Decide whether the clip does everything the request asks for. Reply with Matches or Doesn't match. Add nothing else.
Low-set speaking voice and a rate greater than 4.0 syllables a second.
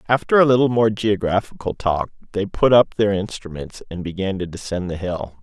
Matches